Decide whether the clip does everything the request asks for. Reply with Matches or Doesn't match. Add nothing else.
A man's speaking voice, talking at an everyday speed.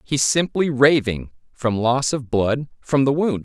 Matches